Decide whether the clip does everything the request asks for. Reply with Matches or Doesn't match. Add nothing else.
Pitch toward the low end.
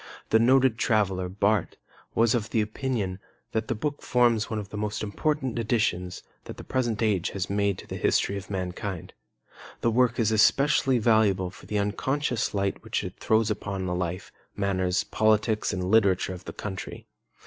Matches